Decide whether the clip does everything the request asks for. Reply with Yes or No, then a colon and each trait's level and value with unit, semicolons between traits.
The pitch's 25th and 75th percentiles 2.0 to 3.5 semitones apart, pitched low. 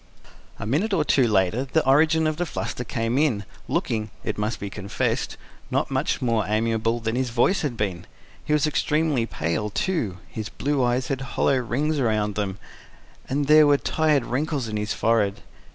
No: wide, 5.5 semitones; low, 120 Hz